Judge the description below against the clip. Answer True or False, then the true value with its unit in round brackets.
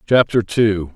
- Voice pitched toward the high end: False (105 Hz)